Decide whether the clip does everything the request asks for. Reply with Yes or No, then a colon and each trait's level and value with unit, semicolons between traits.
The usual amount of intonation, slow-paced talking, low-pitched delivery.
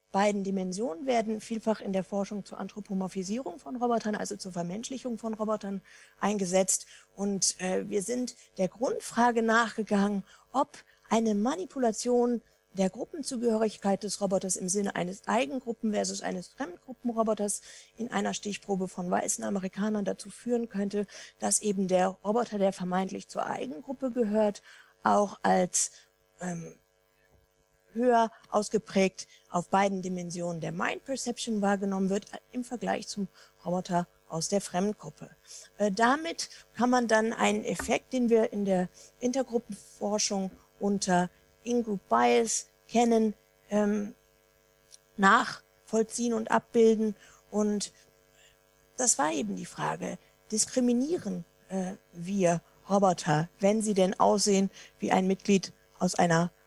No: average, 3.6 semitones; slow, 120 wpm; high, 205 Hz